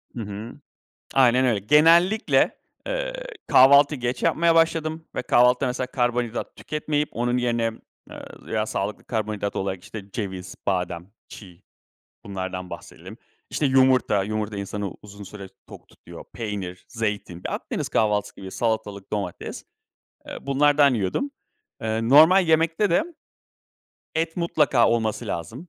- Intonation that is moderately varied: No, wide, 6.1 semitones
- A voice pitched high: No, low, 115 Hz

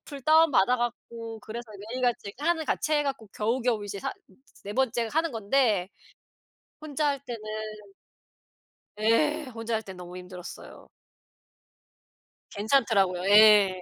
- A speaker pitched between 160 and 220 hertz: No, high, 230 Hz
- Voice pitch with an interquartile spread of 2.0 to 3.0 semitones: No, average, 5.1 semitones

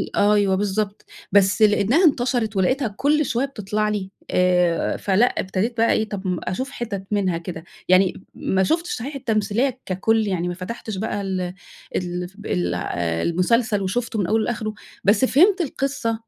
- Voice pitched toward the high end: Yes, high, 205 Hz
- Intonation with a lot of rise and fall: No, average, 4.0 semitones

